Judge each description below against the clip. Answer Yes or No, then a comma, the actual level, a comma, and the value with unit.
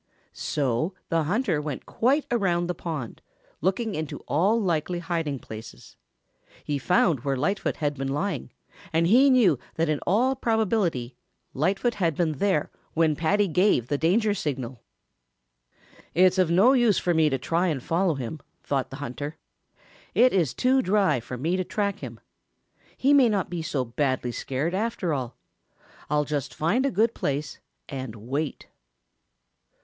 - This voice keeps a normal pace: Yes, average, 155 wpm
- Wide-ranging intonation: Yes, wide, 5.9 semitones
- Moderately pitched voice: Yes, medium, 165 Hz